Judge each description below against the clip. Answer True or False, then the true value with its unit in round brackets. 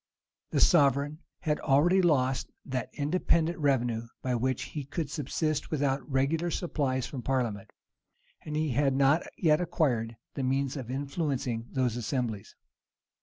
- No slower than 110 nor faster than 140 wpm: True (135 wpm)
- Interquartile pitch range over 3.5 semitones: False (3.2 semitones)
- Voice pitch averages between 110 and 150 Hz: True (140 Hz)